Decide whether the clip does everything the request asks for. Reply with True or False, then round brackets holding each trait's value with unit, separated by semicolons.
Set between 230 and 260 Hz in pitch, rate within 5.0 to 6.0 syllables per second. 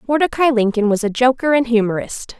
True (240 Hz; 5.8 syllables/s)